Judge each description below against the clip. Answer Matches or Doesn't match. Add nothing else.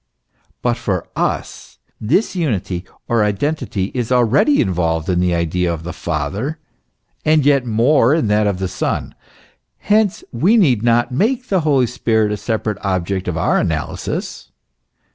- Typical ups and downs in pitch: Doesn't match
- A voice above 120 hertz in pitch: Doesn't match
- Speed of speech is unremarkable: Matches